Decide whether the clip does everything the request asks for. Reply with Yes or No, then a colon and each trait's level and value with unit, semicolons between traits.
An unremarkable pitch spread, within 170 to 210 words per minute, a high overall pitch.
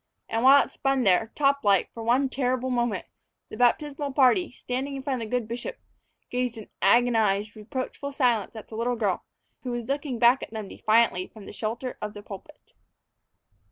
Yes: average, 3.4 semitones; average, 190 wpm; high, 245 Hz